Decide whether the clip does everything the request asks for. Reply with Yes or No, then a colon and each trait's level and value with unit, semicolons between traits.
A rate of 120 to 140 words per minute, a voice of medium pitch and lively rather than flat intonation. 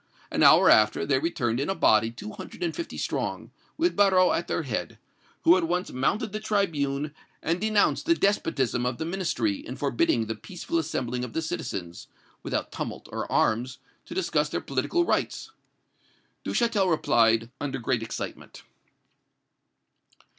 No: average, 155 wpm; medium, 150 Hz; wide, 8.0 semitones